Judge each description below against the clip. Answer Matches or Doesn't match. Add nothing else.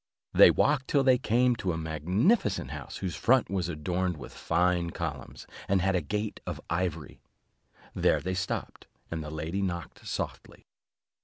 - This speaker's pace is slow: Doesn't match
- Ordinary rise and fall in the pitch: Matches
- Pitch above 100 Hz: Doesn't match